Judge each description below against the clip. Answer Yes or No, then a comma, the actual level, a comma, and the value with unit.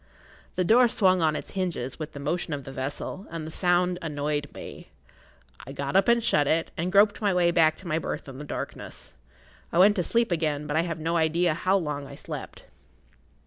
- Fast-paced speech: Yes, fast, 215 wpm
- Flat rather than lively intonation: No, average, 3.6 semitones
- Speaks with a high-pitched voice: No, medium, 165 Hz